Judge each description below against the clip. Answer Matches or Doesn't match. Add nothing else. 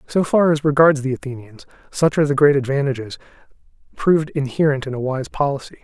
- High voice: Doesn't match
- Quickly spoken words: Doesn't match